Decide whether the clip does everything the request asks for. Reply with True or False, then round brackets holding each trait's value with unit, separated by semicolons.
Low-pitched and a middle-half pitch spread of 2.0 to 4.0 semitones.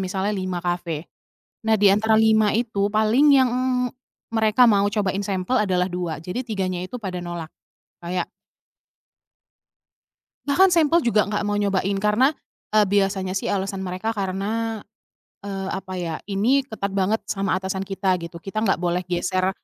False (195 Hz; 2.7 semitones)